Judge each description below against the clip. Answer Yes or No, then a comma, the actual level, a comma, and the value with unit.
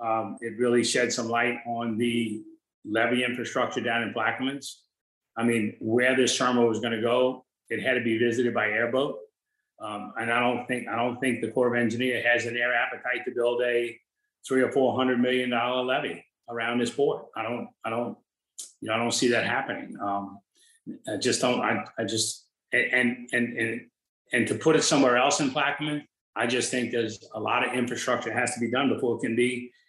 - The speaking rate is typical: No, fast, 210 wpm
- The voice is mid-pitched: No, low, 120 Hz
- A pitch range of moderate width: No, narrow, 1.4 semitones